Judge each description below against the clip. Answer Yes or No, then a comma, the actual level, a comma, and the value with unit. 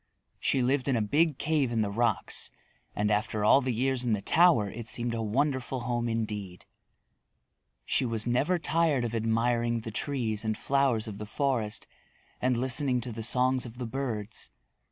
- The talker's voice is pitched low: Yes, low, 120 Hz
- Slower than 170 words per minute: No, average, 175 wpm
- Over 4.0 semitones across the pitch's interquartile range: No, average, 3.2 semitones